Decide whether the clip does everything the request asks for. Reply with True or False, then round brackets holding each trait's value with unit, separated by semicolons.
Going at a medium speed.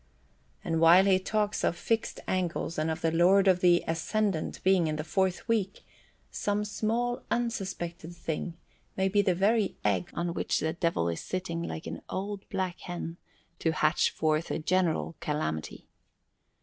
True (160 wpm)